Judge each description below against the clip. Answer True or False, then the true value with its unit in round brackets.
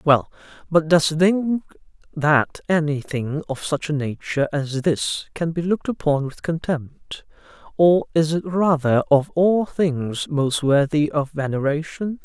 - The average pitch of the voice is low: False (155 Hz)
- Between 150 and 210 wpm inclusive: False (140 wpm)